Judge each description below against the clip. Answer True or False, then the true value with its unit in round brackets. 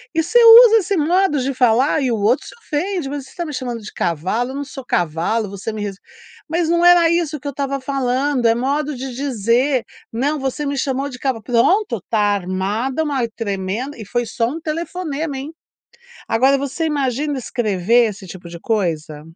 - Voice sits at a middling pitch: False (265 Hz)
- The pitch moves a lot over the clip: False (4.8 semitones)